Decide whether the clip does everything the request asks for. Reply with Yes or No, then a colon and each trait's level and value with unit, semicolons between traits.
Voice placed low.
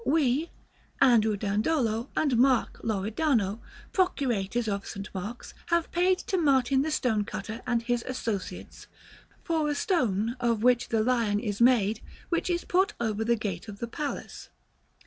No: high, 235 Hz